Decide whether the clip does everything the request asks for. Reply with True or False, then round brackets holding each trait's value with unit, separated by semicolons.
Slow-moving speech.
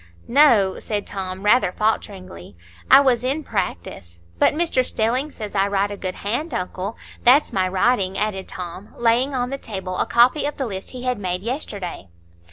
False (175 wpm)